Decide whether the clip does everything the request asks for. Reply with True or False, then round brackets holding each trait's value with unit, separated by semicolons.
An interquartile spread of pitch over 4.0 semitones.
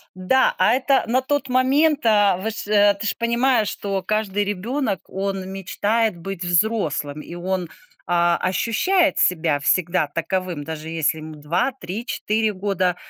True (4.7 semitones)